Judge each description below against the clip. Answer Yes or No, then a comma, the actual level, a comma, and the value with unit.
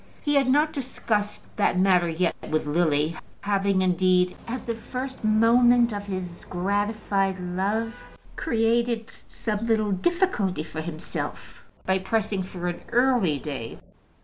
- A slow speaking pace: Yes, slow, 130 wpm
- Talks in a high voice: Yes, high, 205 Hz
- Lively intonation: No, average, 4.3 semitones